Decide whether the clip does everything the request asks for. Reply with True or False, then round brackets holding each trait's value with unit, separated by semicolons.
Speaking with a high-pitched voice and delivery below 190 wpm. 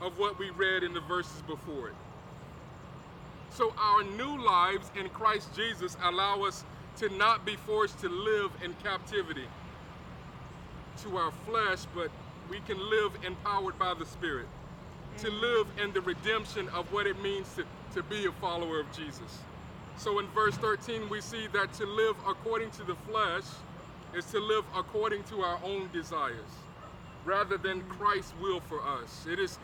True (200 Hz; 165 wpm)